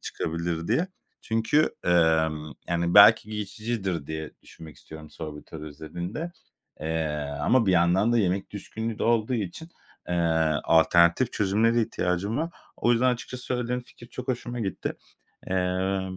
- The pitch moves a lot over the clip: Yes, wide, 6.0 semitones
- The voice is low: Yes, very low, 95 Hz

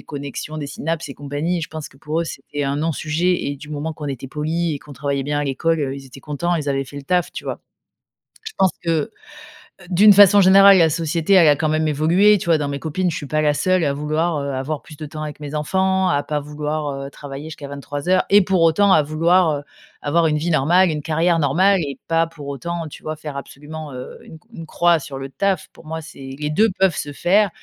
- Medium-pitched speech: Yes, medium, 155 Hz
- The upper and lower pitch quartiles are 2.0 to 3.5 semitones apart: Yes, average, 3.0 semitones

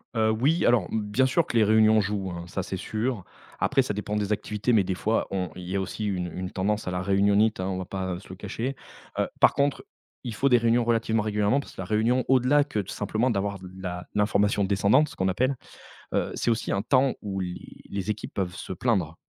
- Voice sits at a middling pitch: No, low, 105 Hz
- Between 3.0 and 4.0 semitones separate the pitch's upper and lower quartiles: Yes, average, 3.3 semitones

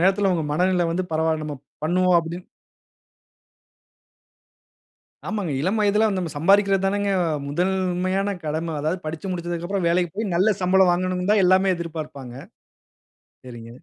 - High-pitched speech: No, medium, 180 Hz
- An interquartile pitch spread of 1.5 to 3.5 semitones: Yes, average, 2.8 semitones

